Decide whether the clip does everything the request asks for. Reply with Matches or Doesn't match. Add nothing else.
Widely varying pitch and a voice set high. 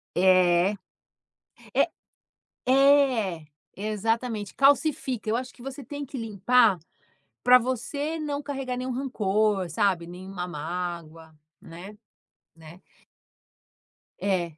Matches